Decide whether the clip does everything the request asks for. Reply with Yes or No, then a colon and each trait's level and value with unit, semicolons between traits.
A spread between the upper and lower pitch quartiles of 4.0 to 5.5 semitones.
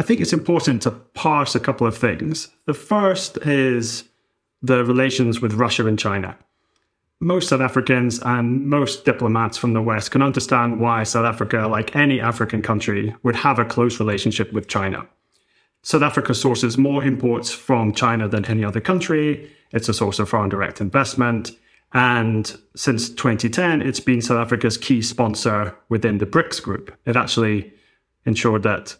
No: average, 3.1 semitones